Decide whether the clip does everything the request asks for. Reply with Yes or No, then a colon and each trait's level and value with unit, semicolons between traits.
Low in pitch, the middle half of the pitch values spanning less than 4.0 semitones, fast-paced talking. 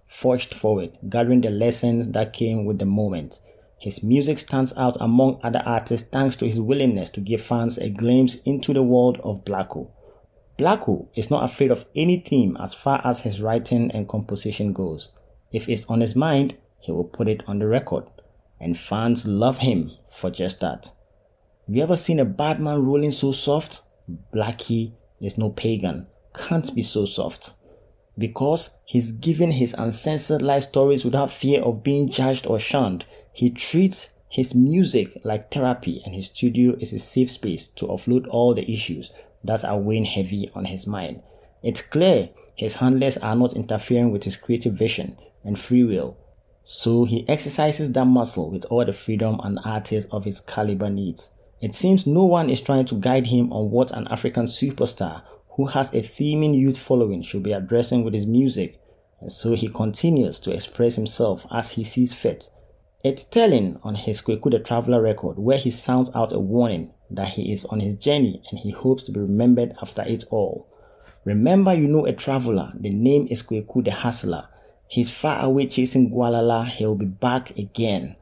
No: low, 120 Hz; average, 3.6 semitones; average, 180 wpm